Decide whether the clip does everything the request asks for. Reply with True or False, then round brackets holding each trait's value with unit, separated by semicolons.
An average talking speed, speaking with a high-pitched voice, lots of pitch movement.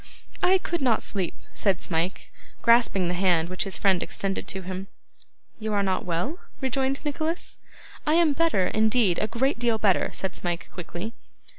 True (165 wpm; 205 Hz; 6.2 semitones)